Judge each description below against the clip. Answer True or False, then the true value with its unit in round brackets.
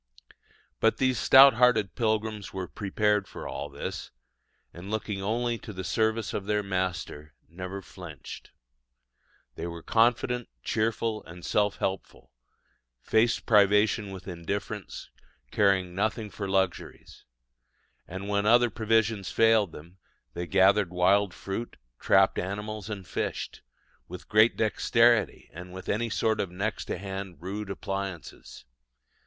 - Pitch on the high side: False (100 Hz)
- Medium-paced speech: False (130 wpm)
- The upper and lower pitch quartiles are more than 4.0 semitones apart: False (2.9 semitones)